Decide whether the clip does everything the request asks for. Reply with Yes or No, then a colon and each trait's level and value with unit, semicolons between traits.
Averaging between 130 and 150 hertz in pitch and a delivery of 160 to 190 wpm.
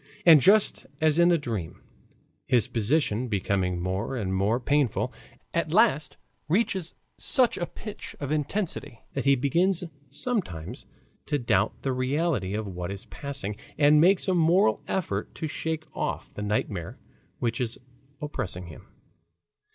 No: low, 135 Hz; average, 145 wpm